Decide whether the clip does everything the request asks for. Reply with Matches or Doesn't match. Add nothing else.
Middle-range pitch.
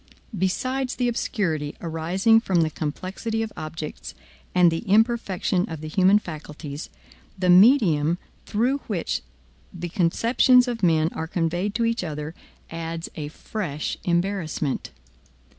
Matches